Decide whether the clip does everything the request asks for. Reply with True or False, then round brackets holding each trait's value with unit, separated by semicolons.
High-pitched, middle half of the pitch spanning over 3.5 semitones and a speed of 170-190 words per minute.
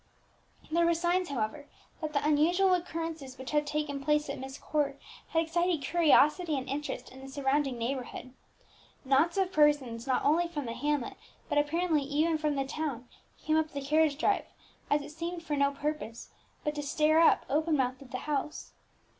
False (295 Hz; 2.8 semitones; 180 wpm)